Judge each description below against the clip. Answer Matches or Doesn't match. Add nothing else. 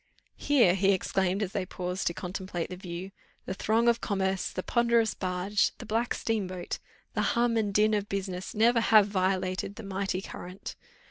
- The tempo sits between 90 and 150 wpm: Doesn't match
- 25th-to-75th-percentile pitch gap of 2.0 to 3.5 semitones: Matches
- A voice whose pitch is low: Doesn't match